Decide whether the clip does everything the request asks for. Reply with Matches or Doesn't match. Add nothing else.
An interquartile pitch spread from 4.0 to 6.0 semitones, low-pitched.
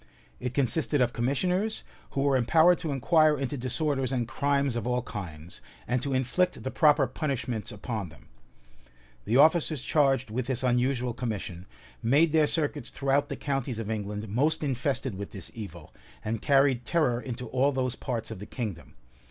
Doesn't match